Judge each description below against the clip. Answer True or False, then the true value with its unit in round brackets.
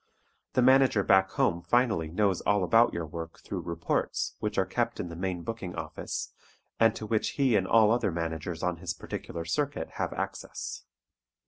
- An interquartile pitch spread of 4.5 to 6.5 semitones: True (5.2 semitones)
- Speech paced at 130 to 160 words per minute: False (180 wpm)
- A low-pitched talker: True (95 Hz)